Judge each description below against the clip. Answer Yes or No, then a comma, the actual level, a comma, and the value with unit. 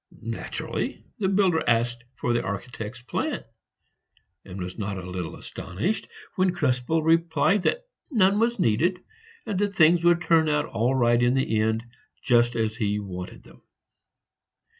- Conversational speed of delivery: Yes, average, 150 wpm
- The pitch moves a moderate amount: No, wide, 7.9 semitones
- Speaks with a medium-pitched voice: No, low, 125 Hz